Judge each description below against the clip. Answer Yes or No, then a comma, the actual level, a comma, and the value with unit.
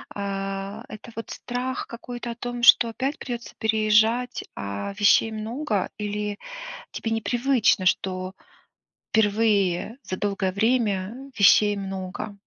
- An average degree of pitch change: Yes, average, 3.2 semitones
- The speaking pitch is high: Yes, high, 215 Hz